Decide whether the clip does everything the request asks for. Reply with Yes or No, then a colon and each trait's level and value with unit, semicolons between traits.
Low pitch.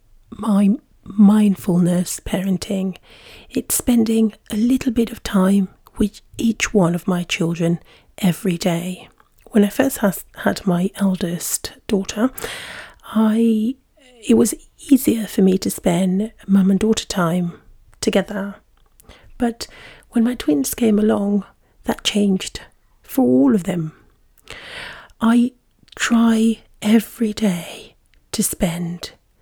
No: high, 205 Hz